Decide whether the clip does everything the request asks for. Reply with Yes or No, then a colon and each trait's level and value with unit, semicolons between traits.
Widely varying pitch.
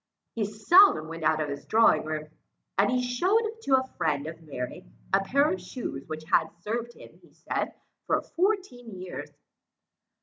Yes: wide, 8.3 semitones